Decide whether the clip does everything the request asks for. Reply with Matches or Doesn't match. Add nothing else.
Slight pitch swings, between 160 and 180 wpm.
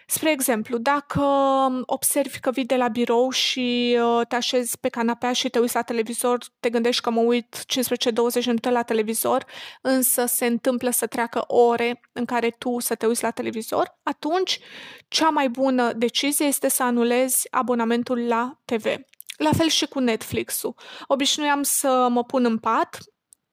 Matches